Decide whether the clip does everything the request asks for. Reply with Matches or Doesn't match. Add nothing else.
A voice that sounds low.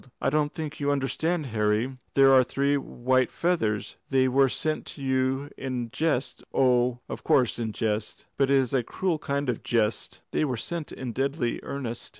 Matches